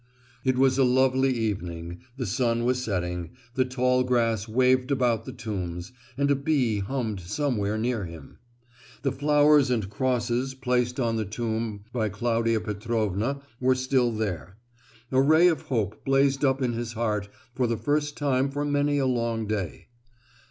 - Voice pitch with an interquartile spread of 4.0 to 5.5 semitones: No, average, 3.5 semitones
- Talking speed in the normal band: Yes, average, 160 wpm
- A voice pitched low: Yes, low, 120 Hz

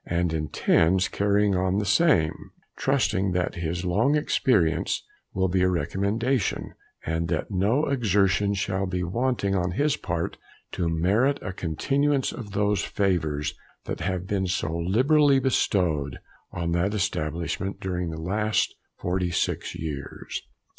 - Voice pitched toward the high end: No, very low, 95 Hz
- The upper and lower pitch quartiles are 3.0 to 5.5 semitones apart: Yes, average, 3.6 semitones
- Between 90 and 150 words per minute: Yes, slow, 135 wpm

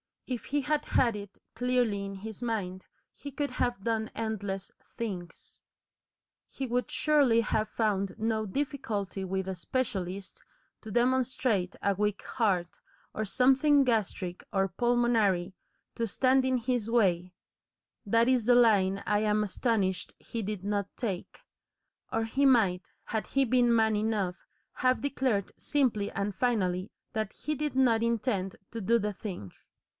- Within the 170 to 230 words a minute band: No, average, 145 wpm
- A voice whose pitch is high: Yes, high, 220 Hz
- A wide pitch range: No, average, 4.0 semitones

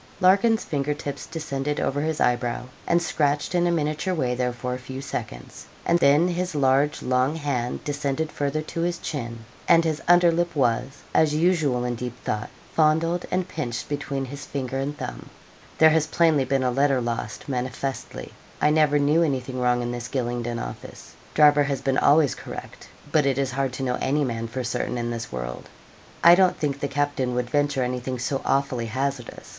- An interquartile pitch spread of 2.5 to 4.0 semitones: Yes, average, 3.6 semitones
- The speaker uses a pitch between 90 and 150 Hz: Yes, medium, 140 Hz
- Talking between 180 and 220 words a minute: Yes, average, 190 wpm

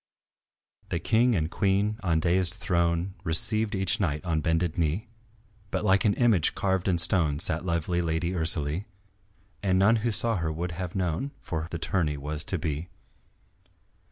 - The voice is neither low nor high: No, very low, 85 Hz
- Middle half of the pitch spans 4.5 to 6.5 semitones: No, average, 3.2 semitones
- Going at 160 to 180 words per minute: Yes, average, 165 wpm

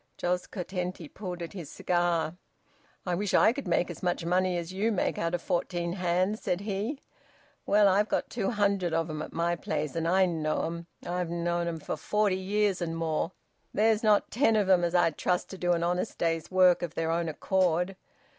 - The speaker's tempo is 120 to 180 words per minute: No, fast, 205 wpm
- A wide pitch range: No, narrow, 2.4 semitones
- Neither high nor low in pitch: Yes, medium, 180 Hz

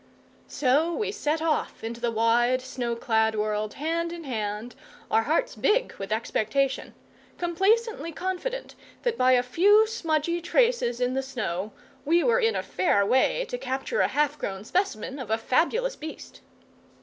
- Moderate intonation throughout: No, wide, 7.2 semitones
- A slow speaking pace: No, average, 160 wpm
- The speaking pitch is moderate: No, very high, 270 Hz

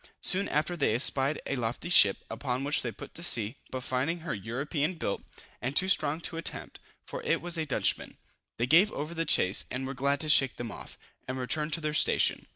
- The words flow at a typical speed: No, fast, 215 wpm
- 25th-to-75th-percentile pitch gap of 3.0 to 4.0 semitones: No, average, 4.5 semitones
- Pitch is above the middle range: No, medium, 145 Hz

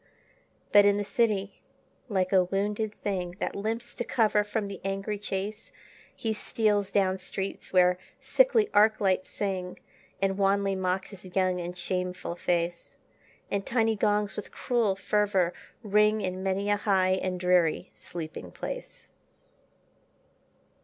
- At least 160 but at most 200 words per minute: No, average, 140 wpm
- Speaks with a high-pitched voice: Yes, high, 195 Hz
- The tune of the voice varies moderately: No, narrow, 2.2 semitones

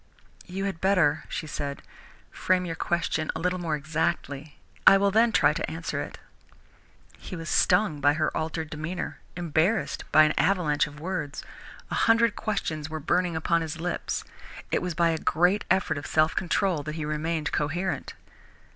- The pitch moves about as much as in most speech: Yes, average, 3.0 semitones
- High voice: No, medium, 165 Hz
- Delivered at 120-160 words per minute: No, average, 170 wpm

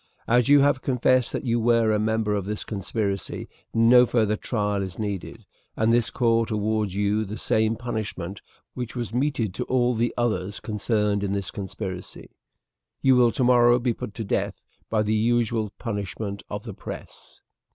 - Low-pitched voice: Yes, low, 110 Hz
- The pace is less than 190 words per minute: Yes, average, 170 wpm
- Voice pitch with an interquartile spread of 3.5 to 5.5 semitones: No, average, 2.7 semitones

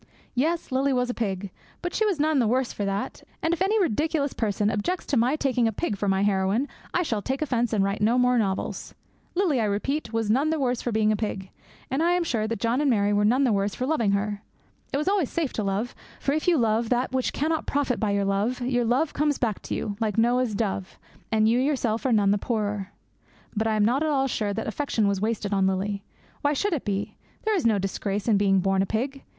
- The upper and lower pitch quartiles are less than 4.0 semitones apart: No, average, 5.1 semitones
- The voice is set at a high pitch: Yes, high, 230 Hz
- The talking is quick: Yes, fast, 245 wpm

